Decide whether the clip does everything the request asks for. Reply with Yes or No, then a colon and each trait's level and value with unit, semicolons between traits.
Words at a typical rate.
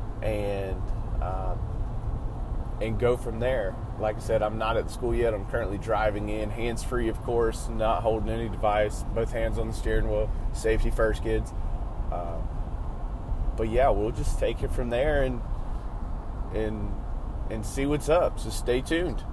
Yes: average, 165 wpm